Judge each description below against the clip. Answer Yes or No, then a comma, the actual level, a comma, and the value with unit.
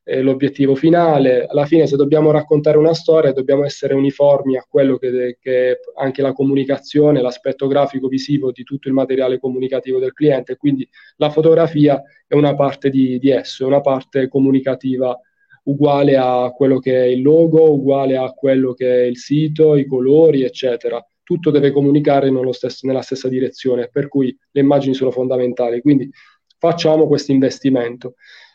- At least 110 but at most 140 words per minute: No, average, 165 wpm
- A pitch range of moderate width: No, narrow, 2.1 semitones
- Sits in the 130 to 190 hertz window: Yes, low, 135 Hz